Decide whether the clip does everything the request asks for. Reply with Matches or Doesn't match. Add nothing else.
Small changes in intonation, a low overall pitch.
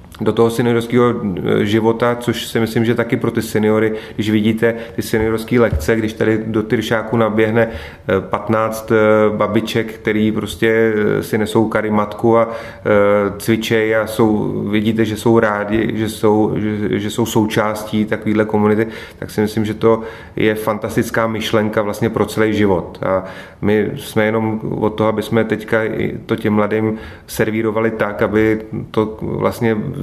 Matches